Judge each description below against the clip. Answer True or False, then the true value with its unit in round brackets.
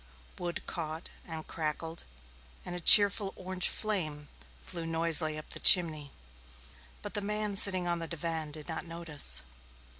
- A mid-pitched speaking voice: True (170 Hz)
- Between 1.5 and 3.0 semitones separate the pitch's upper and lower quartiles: True (2.6 semitones)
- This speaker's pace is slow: False (145 wpm)